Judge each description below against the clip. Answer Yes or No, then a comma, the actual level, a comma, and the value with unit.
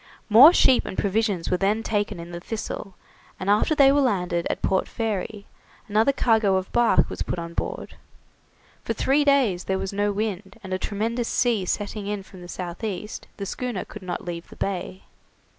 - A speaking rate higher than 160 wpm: Yes, average, 190 wpm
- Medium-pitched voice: No, high, 205 Hz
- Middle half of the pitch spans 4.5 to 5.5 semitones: No, average, 3.2 semitones